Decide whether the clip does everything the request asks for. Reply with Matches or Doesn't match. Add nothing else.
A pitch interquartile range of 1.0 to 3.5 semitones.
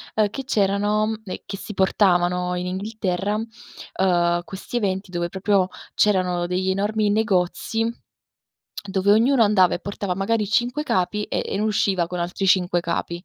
Matches